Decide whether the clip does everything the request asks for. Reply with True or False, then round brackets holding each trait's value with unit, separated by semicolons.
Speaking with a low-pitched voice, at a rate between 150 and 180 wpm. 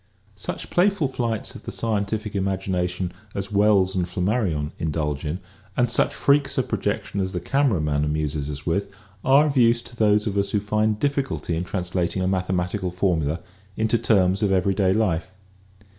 True (95 Hz; 170 wpm)